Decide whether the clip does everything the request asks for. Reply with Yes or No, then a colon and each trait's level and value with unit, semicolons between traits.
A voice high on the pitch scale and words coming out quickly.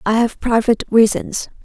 No: high, 225 Hz; average, 145 wpm